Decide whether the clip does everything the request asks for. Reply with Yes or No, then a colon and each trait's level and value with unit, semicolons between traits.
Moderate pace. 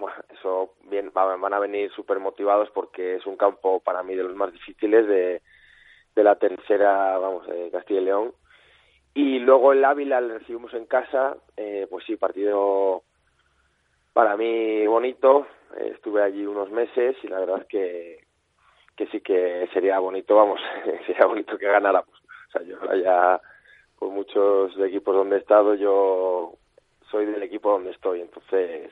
Yes: average, 165 wpm